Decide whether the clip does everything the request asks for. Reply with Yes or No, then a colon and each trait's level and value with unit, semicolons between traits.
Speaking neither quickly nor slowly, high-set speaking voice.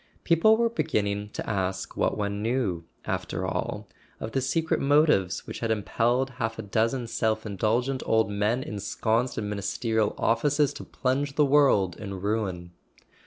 No: average, 155 wpm; low, 110 Hz